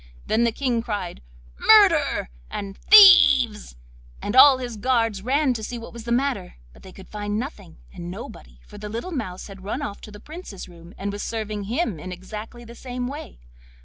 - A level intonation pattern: No, average, 4.4 semitones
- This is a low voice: No, high, 225 Hz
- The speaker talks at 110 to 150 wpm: No, average, 195 wpm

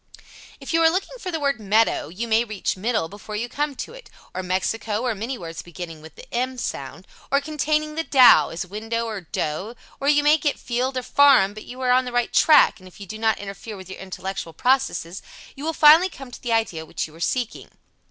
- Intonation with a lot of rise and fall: Yes, wide, 6.3 semitones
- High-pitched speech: Yes, high, 230 Hz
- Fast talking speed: Yes, fast, 230 wpm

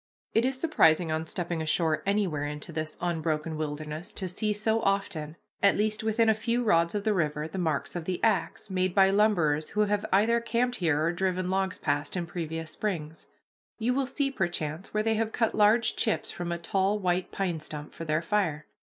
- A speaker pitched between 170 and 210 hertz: Yes, medium, 185 Hz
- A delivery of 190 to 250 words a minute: Yes, average, 200 wpm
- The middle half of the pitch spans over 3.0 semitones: Yes, average, 5.0 semitones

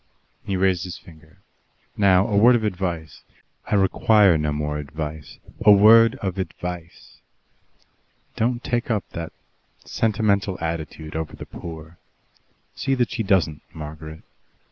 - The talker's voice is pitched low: Yes, very low, 90 Hz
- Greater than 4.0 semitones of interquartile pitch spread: Yes, average, 4.8 semitones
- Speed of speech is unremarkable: No, slow, 130 wpm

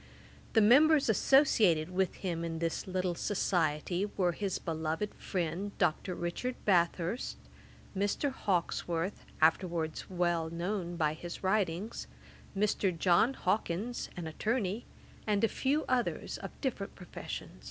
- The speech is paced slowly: Yes, slow, 120 wpm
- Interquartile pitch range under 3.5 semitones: No, average, 3.9 semitones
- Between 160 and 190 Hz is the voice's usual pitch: Yes, medium, 185 Hz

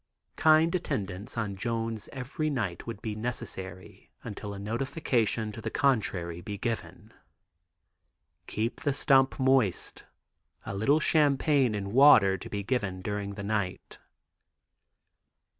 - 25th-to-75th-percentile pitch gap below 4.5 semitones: No, average, 5.1 semitones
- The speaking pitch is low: Yes, low, 110 Hz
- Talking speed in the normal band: No, slow, 125 wpm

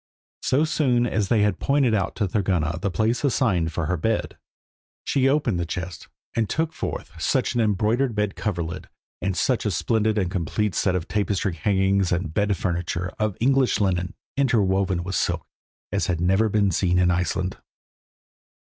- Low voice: Yes, low, 100 Hz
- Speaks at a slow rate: No, average, 170 wpm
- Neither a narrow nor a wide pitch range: Yes, average, 4.0 semitones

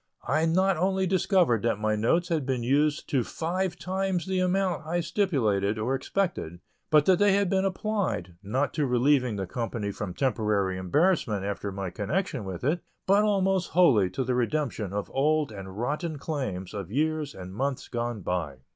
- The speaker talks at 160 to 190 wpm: Yes, average, 175 wpm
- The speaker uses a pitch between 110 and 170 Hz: Yes, medium, 140 Hz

